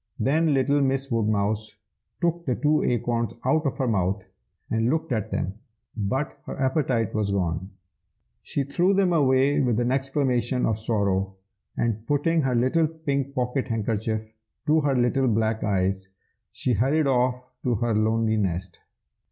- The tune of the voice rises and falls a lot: No, average, 4.3 semitones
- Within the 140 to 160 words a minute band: Yes, average, 155 wpm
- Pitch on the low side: Yes, low, 125 Hz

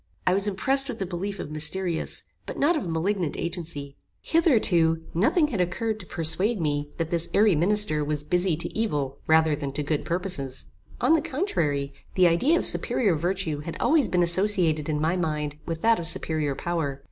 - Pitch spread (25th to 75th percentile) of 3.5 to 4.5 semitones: No, average, 5.0 semitones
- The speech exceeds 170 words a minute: Yes, average, 185 wpm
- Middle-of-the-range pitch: Yes, medium, 170 Hz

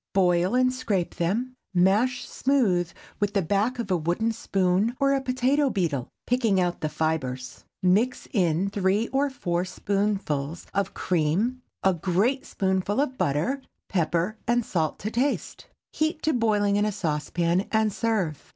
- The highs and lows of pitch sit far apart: Yes, wide, 5.7 semitones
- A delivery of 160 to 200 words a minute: No, average, 150 wpm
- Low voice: No, high, 200 Hz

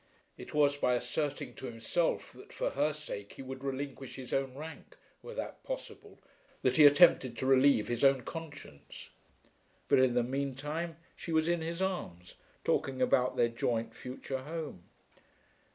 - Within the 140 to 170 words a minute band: Yes, average, 165 wpm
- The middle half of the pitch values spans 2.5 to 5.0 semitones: Yes, average, 3.5 semitones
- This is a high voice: No, low, 135 Hz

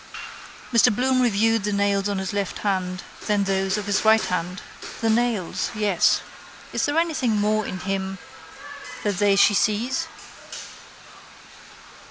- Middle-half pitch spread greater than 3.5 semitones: No, narrow, 2.5 semitones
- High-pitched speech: Yes, high, 205 Hz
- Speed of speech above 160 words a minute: No, average, 140 wpm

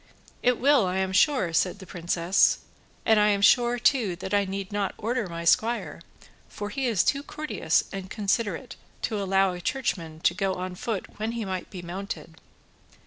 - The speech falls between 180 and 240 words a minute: Yes, average, 185 wpm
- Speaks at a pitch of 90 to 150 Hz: No, high, 200 Hz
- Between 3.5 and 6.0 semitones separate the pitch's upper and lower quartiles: Yes, average, 3.8 semitones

